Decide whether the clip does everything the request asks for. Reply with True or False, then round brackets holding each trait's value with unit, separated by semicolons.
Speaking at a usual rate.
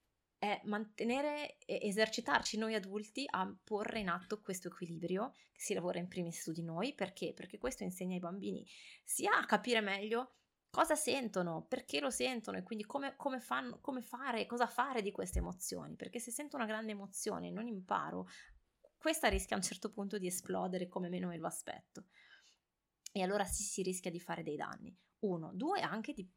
False (185 wpm)